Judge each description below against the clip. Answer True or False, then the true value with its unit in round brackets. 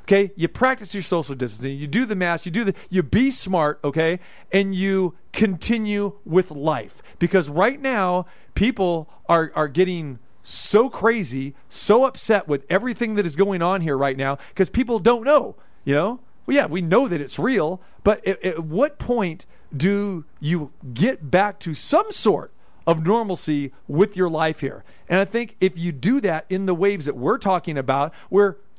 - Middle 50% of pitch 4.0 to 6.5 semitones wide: True (4.4 semitones)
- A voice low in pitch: False (185 Hz)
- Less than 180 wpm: False (185 wpm)